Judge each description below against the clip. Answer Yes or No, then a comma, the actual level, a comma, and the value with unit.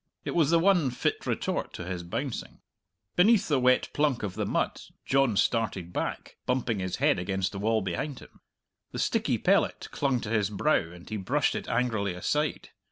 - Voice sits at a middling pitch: No, low, 115 Hz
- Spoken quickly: No, average, 185 wpm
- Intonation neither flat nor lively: No, wide, 6.2 semitones